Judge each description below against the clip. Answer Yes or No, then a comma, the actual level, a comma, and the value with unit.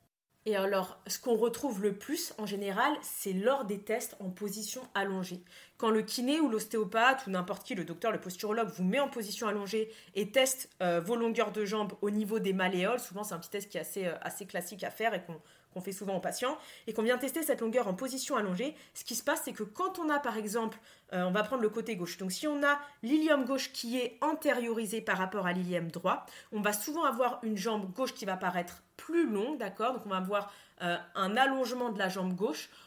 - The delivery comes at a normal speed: No, fast, 235 wpm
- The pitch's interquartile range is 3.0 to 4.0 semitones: No, average, 4.8 semitones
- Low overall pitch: No, high, 215 Hz